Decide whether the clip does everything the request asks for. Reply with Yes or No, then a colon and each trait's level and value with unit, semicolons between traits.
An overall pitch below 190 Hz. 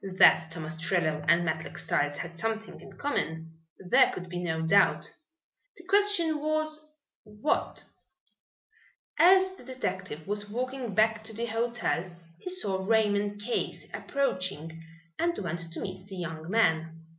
No: high, 200 Hz